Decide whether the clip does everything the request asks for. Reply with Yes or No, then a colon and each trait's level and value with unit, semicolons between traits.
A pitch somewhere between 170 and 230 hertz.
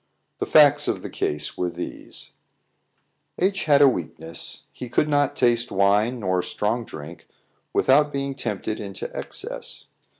No: low, 120 Hz